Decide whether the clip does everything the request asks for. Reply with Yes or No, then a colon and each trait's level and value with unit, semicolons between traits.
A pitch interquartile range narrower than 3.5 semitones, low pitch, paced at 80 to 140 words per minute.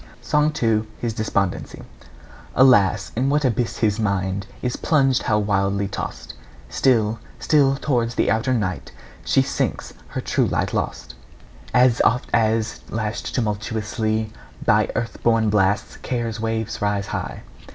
Yes: average, 2.9 semitones; low, 110 Hz; slow, 135 wpm